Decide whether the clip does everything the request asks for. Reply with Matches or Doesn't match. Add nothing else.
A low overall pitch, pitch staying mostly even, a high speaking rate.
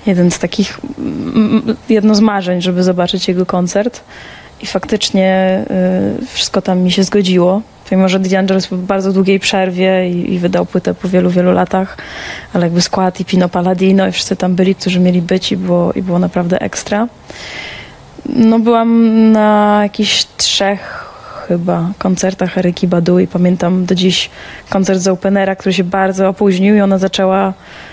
Doesn't match